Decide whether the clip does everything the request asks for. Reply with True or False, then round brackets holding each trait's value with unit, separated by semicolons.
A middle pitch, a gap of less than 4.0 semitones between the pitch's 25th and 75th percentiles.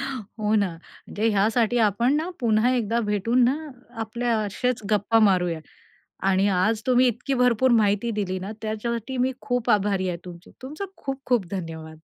False (220 Hz; 3.6 semitones)